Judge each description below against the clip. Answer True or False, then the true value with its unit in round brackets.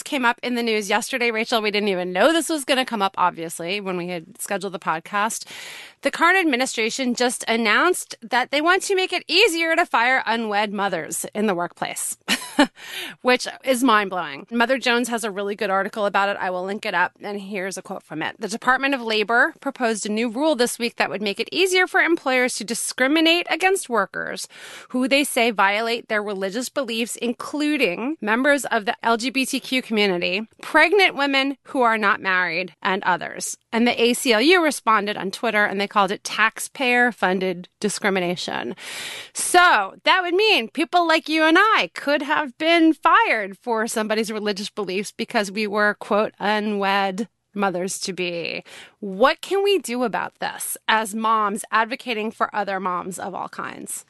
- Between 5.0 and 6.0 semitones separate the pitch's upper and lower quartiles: True (5.4 semitones)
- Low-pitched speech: False (230 Hz)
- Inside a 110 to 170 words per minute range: False (180 wpm)